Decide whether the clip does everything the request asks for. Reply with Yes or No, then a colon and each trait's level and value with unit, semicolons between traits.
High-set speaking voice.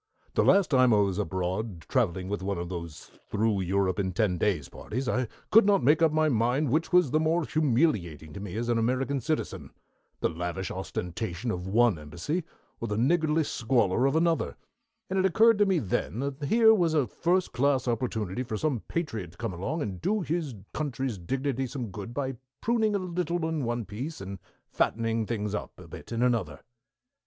No: low, 120 Hz